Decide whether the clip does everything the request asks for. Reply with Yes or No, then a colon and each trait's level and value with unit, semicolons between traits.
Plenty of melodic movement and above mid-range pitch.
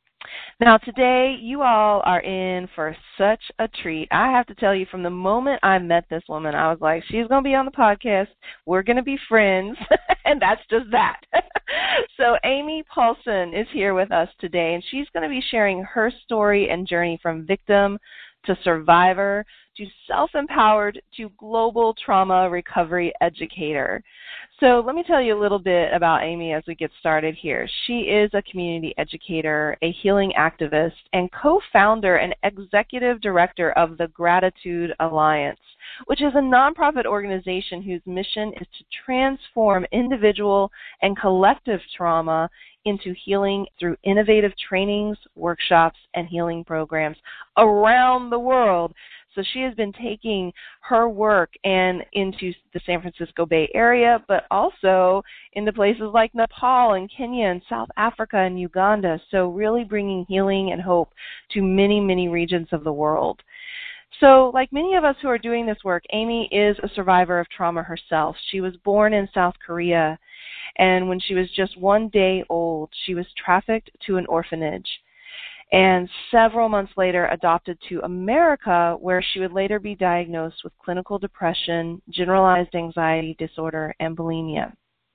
No: average, 4.5 semitones; high, 195 Hz